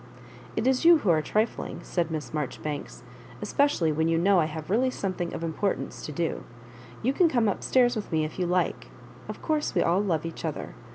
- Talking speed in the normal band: No, fast, 225 wpm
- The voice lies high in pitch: No, medium, 175 Hz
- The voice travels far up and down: Yes, wide, 6.7 semitones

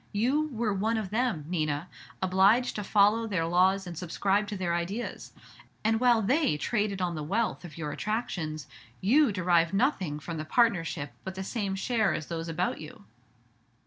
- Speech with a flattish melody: No, average, 4.7 semitones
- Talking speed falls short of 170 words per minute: No, average, 175 wpm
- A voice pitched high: Yes, high, 195 Hz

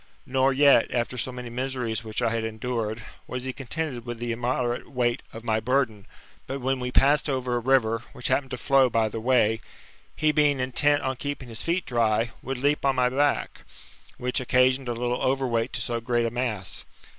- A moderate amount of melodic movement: No, narrow, 2.3 semitones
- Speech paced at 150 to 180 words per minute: No, average, 200 wpm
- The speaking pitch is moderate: No, low, 125 Hz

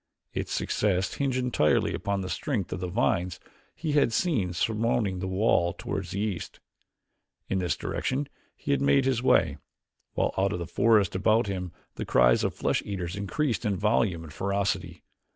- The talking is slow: No, average, 175 wpm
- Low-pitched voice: Yes, low, 100 Hz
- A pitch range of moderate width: Yes, average, 4.2 semitones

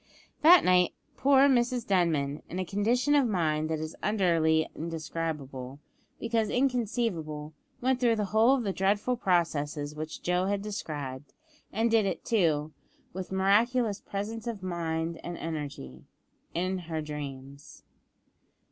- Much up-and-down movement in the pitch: Yes, wide, 6.2 semitones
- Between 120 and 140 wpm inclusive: Yes, slow, 135 wpm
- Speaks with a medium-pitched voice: Yes, medium, 180 Hz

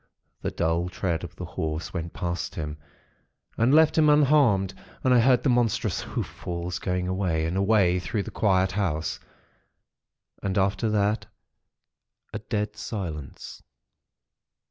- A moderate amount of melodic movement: Yes, average, 4.1 semitones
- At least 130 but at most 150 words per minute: Yes, average, 140 wpm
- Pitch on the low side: Yes, very low, 95 Hz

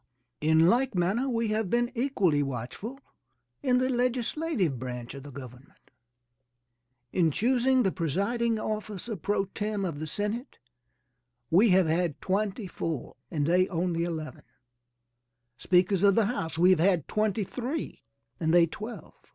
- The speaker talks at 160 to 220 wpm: No, average, 145 wpm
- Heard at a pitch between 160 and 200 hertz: Yes, high, 190 Hz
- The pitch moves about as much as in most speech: No, wide, 6.0 semitones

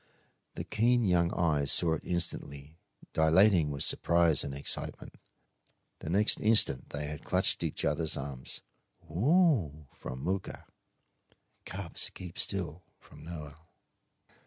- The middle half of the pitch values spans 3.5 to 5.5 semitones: Yes, average, 4.1 semitones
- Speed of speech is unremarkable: No, slow, 120 wpm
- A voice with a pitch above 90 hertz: No, very low, 85 Hz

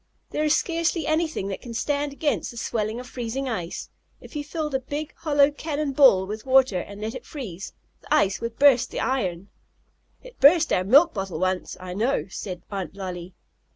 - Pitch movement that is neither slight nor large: No, wide, 7.0 semitones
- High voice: Yes, very high, 250 Hz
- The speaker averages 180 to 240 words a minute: Yes, average, 190 wpm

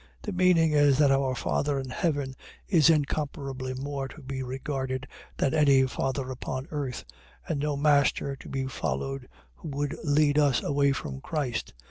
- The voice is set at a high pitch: No, medium, 140 Hz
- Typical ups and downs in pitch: No, narrow, 1.9 semitones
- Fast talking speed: No, average, 160 wpm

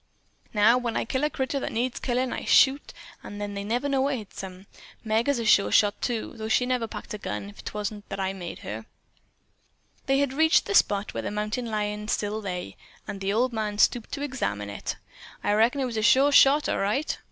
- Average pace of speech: No, fast, 220 wpm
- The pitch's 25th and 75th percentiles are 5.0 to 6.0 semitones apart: No, average, 4.0 semitones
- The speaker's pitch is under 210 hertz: No, high, 220 Hz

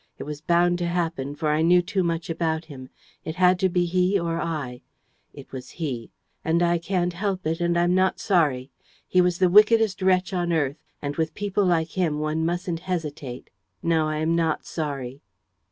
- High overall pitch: No, medium, 170 Hz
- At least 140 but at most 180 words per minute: No, average, 195 wpm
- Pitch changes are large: No, average, 2.7 semitones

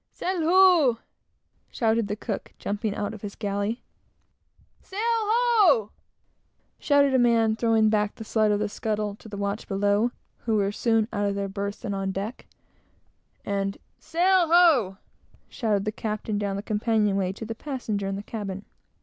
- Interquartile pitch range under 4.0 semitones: Yes, average, 3.3 semitones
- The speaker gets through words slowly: No, average, 165 wpm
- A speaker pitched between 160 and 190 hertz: No, high, 215 Hz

